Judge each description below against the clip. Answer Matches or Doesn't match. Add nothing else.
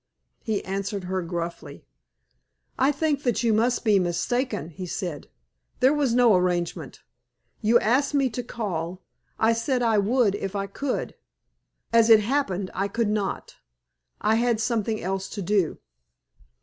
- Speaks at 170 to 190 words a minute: Doesn't match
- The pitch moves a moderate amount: Matches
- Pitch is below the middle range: Doesn't match